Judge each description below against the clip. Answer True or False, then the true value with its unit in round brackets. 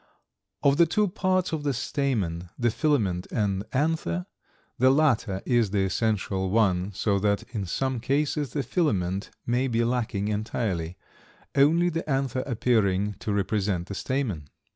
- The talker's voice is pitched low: True (115 Hz)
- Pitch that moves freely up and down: True (6.1 semitones)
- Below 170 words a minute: True (145 wpm)